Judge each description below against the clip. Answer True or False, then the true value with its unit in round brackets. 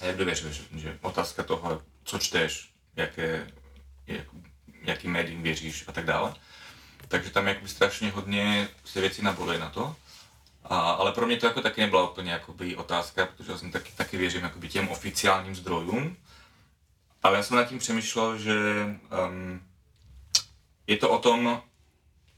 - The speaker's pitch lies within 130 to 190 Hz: False (90 Hz)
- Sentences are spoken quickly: False (155 wpm)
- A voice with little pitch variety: False (3.9 semitones)